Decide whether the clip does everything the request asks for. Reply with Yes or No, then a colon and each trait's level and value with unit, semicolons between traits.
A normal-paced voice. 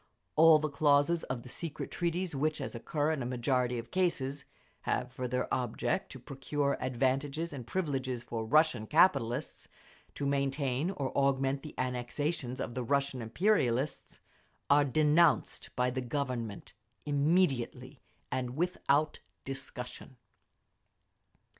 No: slow, 130 wpm